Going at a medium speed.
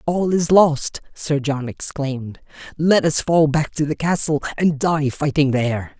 Yes: average, 170 wpm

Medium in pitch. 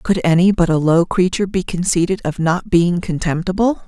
Yes: medium, 180 Hz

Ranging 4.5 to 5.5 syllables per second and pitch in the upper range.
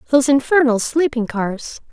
Yes: 5.0 syllables/s; very high, 260 Hz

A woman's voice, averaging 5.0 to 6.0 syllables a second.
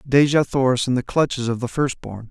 No: male; 5.5 syllables/s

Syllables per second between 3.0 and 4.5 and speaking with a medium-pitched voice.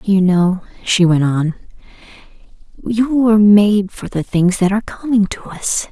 No: 4.4 syllables/s; high, 200 Hz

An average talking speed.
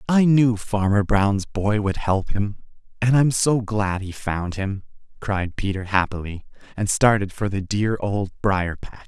Yes: average, 170 wpm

